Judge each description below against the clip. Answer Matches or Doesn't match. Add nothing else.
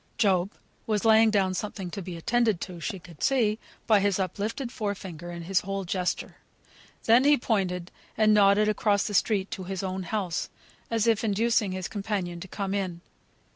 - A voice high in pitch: Matches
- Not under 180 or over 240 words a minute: Matches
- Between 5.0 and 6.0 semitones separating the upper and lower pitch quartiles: Doesn't match